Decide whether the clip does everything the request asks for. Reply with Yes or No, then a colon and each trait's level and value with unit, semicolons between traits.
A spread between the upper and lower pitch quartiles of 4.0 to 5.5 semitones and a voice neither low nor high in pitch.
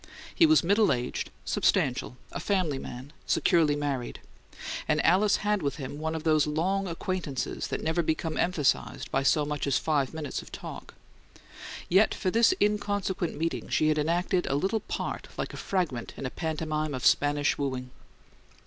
Yes: average, 4.3 semitones; medium, 155 Hz